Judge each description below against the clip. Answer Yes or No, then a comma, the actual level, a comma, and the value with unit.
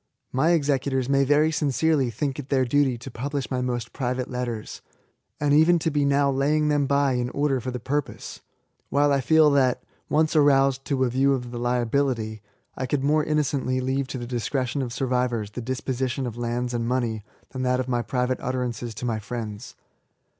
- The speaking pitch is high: No, low, 130 Hz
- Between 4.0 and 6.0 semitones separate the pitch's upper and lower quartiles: No, narrow, 2.6 semitones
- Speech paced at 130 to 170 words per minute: No, average, 195 wpm